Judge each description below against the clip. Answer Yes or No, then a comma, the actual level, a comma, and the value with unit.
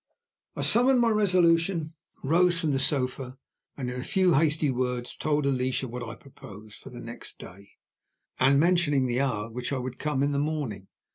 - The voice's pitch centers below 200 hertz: Yes, medium, 140 Hz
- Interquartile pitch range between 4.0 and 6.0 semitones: Yes, average, 4.6 semitones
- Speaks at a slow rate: No, average, 190 wpm